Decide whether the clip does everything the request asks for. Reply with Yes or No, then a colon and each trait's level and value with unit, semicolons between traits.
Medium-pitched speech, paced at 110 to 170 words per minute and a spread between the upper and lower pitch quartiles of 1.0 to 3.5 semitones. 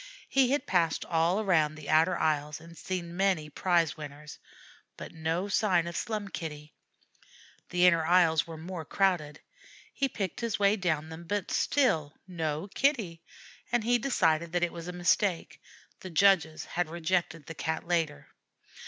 Yes: medium, 170 Hz; average, 160 wpm; average, 3.2 semitones